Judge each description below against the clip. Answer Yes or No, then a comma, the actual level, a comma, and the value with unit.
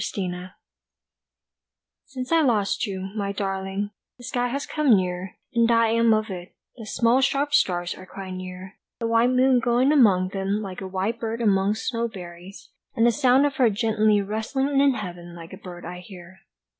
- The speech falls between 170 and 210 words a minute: Yes, average, 180 wpm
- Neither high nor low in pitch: No, high, 210 Hz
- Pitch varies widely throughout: No, average, 4.3 semitones